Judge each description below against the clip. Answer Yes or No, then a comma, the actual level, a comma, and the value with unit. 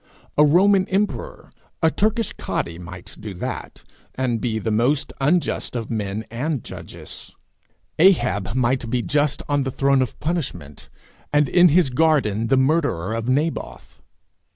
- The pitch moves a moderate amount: No, wide, 5.9 semitones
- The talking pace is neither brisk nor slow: Yes, average, 150 wpm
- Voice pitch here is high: No, low, 130 Hz